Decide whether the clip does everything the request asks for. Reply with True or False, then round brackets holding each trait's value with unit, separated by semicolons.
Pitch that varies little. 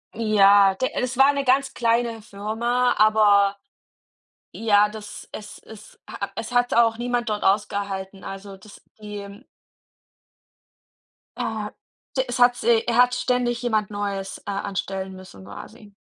False (3.2 semitones)